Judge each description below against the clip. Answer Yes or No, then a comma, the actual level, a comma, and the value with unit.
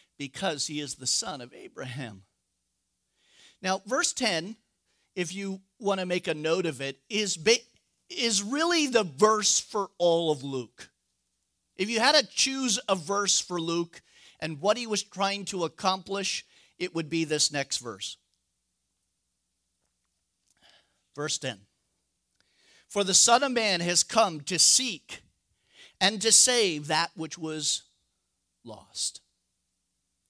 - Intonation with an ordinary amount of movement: No, wide, 6.4 semitones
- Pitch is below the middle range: No, medium, 175 Hz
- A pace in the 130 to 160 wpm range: Yes, slow, 135 wpm